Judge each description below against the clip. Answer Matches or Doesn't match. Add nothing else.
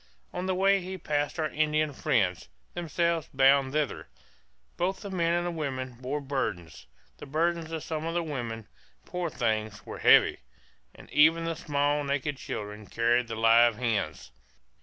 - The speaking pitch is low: Doesn't match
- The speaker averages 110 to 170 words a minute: Matches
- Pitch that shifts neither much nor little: Doesn't match